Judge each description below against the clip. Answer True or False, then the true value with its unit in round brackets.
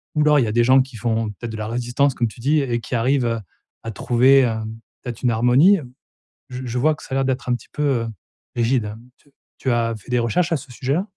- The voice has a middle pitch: False (125 Hz)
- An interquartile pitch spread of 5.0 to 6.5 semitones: False (2.8 semitones)